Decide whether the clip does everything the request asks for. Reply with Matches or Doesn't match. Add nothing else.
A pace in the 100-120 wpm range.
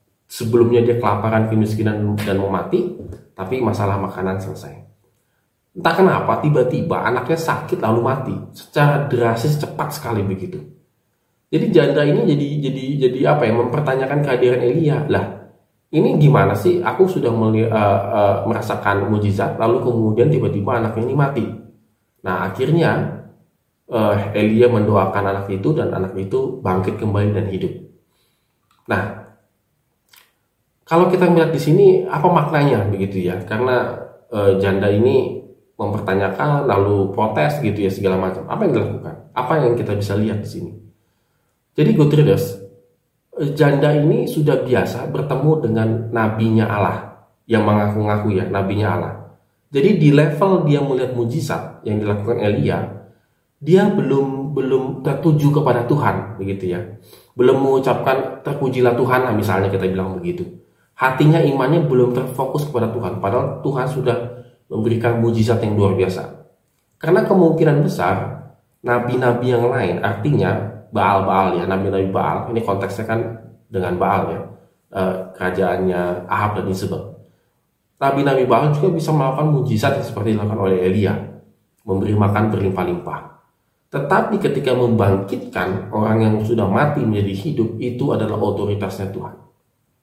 Doesn't match